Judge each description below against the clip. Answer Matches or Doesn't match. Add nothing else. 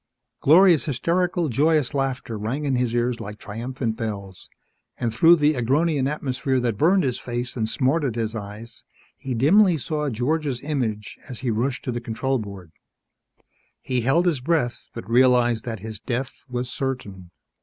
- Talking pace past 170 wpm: Doesn't match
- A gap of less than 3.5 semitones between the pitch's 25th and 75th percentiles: Doesn't match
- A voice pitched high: Doesn't match